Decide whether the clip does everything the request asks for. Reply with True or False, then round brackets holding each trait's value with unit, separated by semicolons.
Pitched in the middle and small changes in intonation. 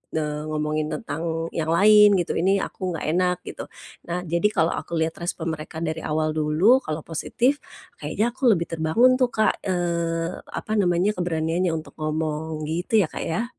False (170 Hz; 3.0 semitones)